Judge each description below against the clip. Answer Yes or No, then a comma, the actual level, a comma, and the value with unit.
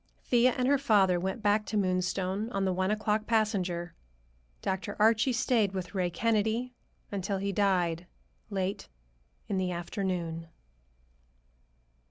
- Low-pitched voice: No, high, 195 Hz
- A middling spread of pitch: Yes, average, 3.0 semitones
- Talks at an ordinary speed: No, slow, 130 wpm